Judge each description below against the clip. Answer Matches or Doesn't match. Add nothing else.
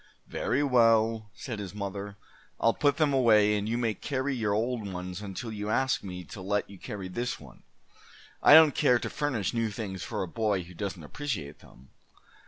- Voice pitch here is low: Matches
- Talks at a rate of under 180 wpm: Doesn't match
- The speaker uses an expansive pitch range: Doesn't match